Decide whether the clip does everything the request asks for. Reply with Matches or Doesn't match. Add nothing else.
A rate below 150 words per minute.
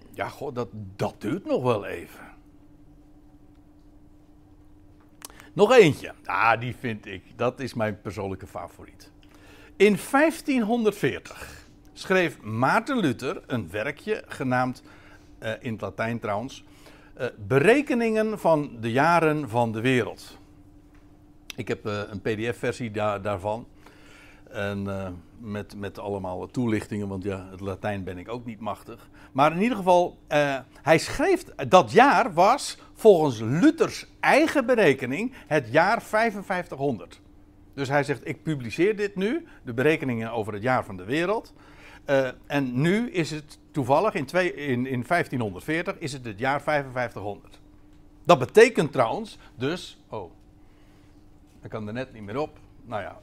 Matches